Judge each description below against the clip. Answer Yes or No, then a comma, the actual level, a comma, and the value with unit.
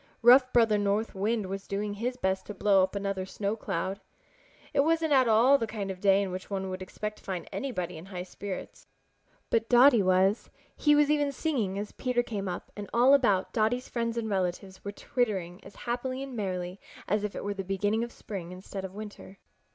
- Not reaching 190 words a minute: No, fast, 205 wpm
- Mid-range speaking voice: No, high, 205 Hz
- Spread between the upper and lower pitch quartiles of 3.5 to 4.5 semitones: Yes, average, 3.9 semitones